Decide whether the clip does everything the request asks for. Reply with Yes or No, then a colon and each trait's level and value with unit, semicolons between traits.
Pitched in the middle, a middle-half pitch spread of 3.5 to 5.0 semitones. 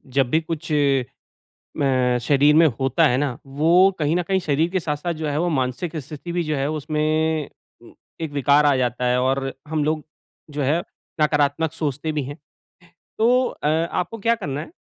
No: medium, 150 Hz; average, 2.8 semitones